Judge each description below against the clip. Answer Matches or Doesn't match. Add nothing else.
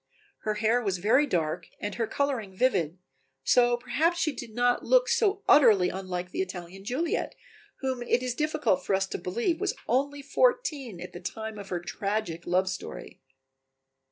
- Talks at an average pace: Matches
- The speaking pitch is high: Matches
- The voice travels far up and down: Matches